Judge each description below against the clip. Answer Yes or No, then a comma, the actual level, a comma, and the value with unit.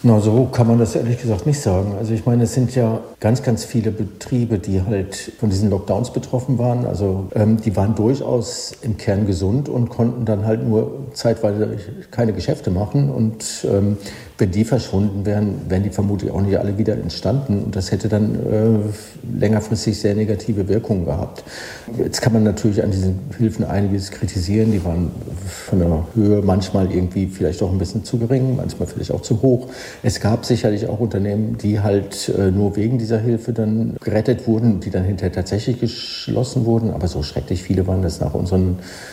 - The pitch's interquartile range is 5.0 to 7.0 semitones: No, average, 2.8 semitones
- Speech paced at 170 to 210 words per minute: Yes, fast, 190 wpm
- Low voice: Yes, low, 110 Hz